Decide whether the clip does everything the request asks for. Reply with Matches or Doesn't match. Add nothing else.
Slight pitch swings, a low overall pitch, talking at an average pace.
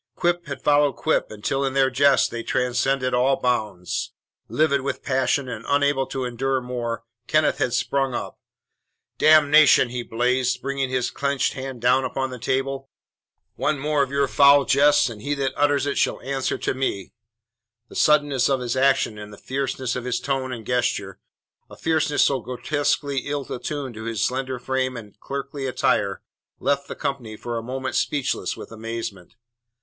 Matches